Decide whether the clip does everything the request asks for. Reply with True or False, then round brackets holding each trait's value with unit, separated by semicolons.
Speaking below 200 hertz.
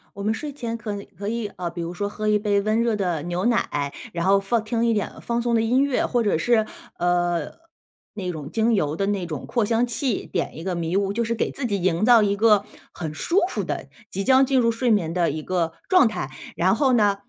False (205 Hz)